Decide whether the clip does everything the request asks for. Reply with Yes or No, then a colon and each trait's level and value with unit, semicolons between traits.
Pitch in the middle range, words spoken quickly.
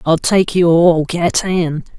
No: medium, 170 Hz; average, 180 wpm